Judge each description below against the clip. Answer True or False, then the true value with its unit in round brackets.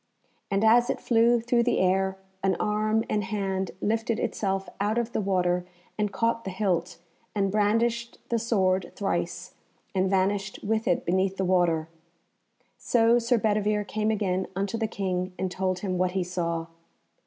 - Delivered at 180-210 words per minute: False (165 wpm)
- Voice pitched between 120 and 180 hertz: False (200 Hz)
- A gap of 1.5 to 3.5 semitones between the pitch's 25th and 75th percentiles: True (2.9 semitones)